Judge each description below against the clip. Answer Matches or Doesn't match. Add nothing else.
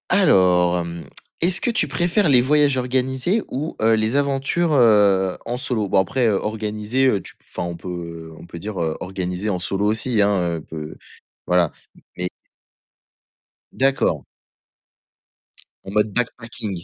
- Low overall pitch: Matches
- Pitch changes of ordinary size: Doesn't match